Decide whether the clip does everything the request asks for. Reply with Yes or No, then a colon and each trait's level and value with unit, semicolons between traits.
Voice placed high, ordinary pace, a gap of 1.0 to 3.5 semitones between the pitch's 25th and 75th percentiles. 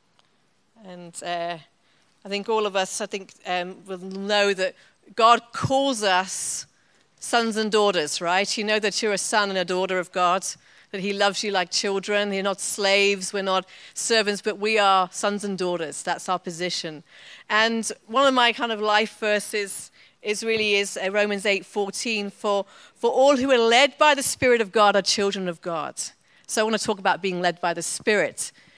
Yes: high, 200 Hz; average, 190 wpm; narrow, 2.5 semitones